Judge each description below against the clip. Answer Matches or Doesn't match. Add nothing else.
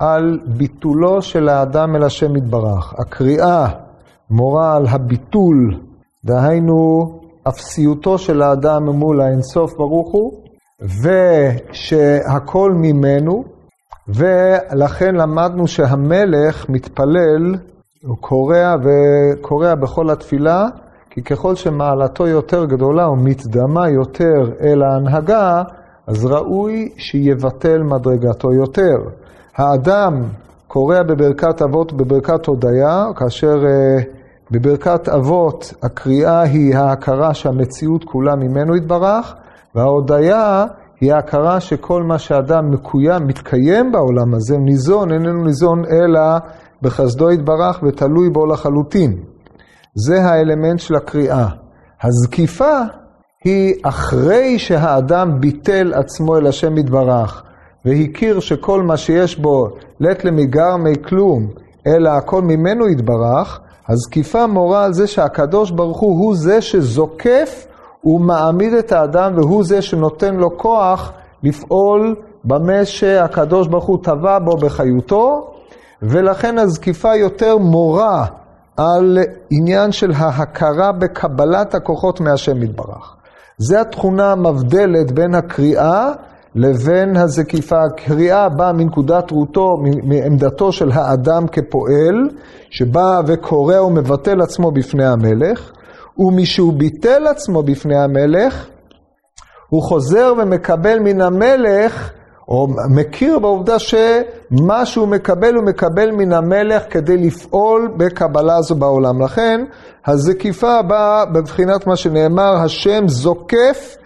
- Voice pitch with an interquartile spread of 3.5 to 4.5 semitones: Doesn't match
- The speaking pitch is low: Doesn't match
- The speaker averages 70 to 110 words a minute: Matches